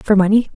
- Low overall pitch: No, high, 205 Hz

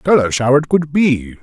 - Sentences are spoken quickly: Yes, fast, 255 wpm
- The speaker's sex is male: Yes, male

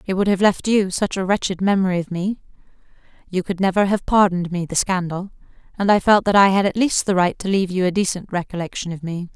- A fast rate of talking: Yes, fast, 230 wpm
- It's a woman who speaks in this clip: Yes, female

